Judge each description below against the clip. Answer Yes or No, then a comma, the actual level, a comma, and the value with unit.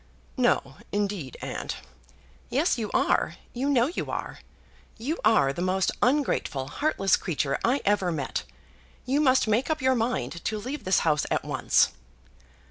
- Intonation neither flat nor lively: No, wide, 6.2 semitones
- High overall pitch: Yes, high, 220 Hz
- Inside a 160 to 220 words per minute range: No, average, 150 wpm